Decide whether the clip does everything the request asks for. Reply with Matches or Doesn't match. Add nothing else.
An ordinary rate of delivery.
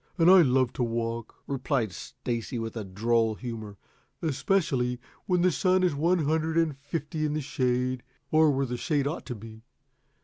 Matches